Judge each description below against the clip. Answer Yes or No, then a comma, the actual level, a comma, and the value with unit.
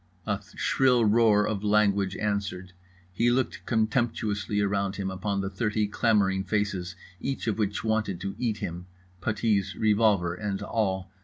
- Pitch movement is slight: Yes, narrow, 2.3 semitones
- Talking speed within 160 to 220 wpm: No, average, 140 wpm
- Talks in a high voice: No, low, 105 Hz